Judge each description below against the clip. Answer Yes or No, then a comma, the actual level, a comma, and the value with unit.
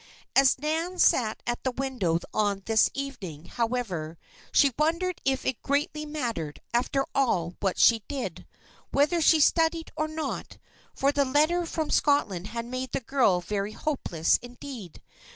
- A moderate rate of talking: Yes, average, 150 wpm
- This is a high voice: Yes, very high, 260 Hz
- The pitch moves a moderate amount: No, wide, 5.8 semitones